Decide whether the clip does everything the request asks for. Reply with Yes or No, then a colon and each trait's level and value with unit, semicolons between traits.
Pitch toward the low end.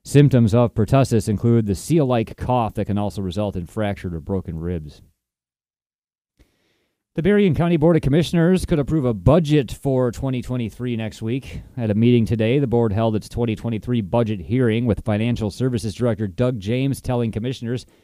Yes: low, 115 Hz